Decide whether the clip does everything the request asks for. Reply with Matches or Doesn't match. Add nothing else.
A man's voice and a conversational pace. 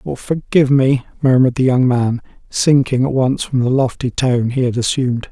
Matches